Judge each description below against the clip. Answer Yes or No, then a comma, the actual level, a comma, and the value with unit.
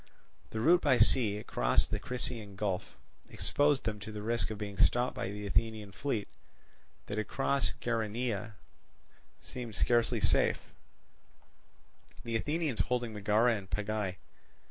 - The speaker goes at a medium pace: No, slow, 130 wpm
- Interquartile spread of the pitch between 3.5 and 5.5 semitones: No, average, 2.8 semitones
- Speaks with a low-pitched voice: Yes, low, 110 Hz